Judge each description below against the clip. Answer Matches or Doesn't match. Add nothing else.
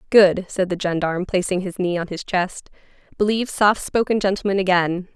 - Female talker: Matches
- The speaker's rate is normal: Matches